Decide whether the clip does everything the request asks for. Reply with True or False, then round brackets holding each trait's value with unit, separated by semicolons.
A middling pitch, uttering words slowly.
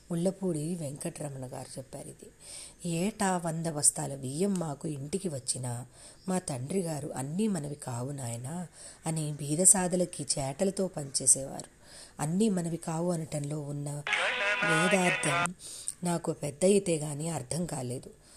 False (160 Hz; 115 wpm)